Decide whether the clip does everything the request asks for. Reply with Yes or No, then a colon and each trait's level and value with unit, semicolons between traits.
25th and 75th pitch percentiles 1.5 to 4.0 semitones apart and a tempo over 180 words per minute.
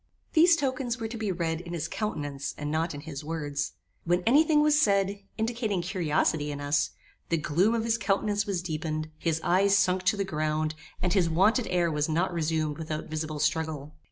No: average, 5.0 semitones; average, 195 wpm